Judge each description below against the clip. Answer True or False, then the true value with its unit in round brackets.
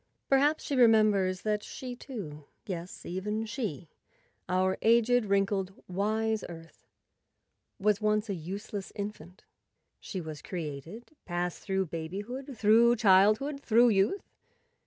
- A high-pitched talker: True (205 Hz)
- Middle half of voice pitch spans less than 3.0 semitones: False (3.4 semitones)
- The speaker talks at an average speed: False (115 wpm)